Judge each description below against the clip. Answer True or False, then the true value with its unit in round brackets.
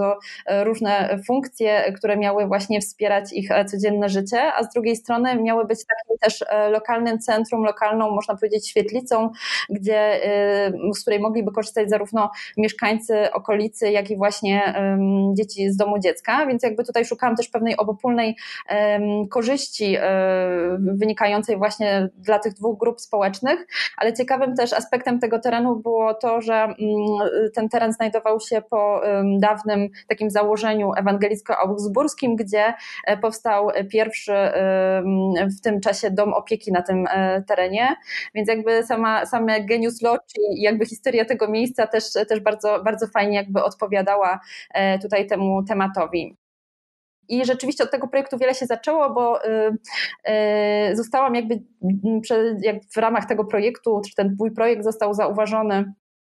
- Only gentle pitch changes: True (2.0 semitones)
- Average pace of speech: True (130 wpm)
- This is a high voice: True (215 Hz)